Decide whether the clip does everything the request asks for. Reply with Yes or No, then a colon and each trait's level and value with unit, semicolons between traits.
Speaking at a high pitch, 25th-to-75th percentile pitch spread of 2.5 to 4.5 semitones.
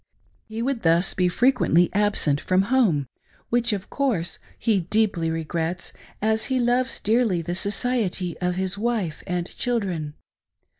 No: high, 195 Hz; average, 5.2 semitones